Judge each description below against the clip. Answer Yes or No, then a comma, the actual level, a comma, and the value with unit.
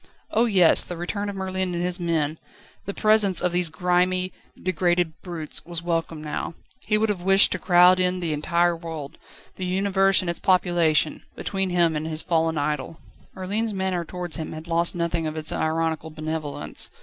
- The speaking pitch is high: No, medium, 175 Hz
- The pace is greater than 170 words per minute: Yes, average, 180 wpm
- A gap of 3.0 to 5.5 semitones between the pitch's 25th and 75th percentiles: No, narrow, 2.5 semitones